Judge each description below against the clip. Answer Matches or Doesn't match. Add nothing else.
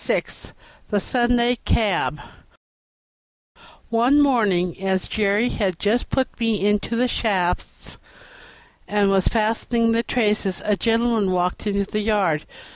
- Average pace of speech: Doesn't match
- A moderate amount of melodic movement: Matches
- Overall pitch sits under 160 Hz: Doesn't match